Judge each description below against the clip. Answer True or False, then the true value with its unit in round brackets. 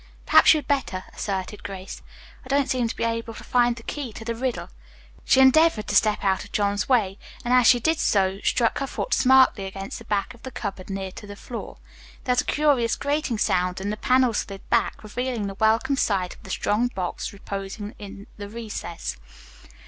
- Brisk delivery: True (210 wpm)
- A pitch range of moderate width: True (4.2 semitones)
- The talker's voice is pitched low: False (220 Hz)